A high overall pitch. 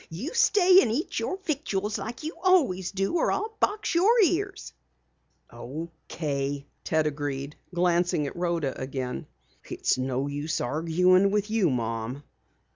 No: medium, 175 Hz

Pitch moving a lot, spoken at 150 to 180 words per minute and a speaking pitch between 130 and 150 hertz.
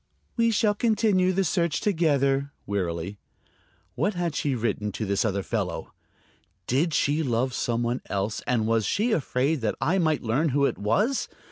Yes: wide, 7.9 semitones; average, 165 wpm; medium, 140 Hz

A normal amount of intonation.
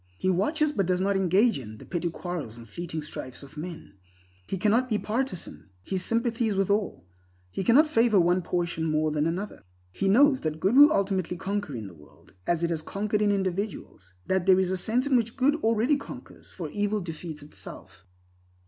Yes: average, 5.0 semitones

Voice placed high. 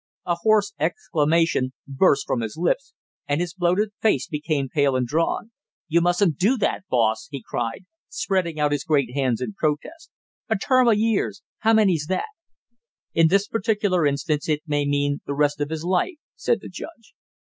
No: medium, 165 Hz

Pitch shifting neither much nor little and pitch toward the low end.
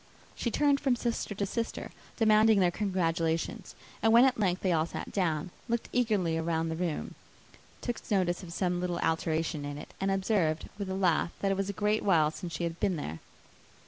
No: average, 4.2 semitones; medium, 185 Hz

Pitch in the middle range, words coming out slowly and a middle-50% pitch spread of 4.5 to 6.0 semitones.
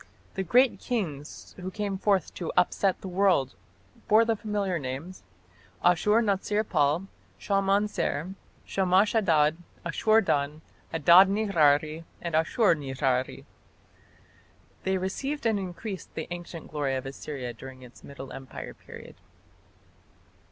Yes: medium, 180 Hz; slow, 120 wpm; average, 5.2 semitones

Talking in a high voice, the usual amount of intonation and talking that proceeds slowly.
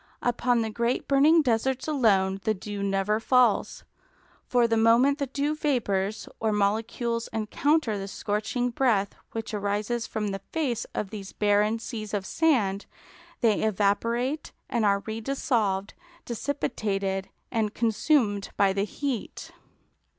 Yes: high, 220 Hz; average, 3.4 semitones; slow, 130 wpm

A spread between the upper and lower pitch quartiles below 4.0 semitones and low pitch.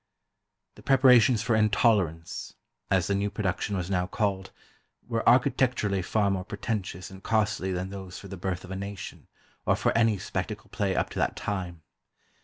Yes: average, 2.8 semitones; low, 100 Hz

